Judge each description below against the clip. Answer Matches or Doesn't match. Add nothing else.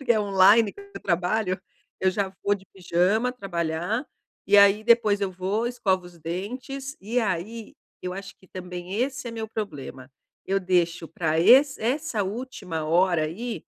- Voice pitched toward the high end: Matches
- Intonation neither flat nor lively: Matches